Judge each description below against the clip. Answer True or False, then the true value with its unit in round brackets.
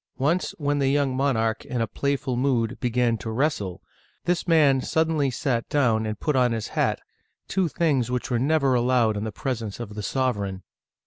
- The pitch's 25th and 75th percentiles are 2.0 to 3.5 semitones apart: False (3.9 semitones)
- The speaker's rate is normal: True (180 wpm)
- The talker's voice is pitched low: True (125 Hz)